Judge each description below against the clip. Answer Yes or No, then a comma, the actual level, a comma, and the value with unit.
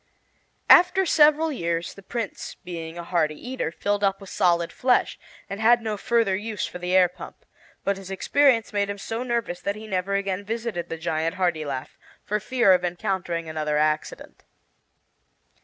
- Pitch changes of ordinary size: Yes, average, 4.7 semitones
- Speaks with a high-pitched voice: Yes, high, 195 Hz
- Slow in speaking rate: No, average, 175 wpm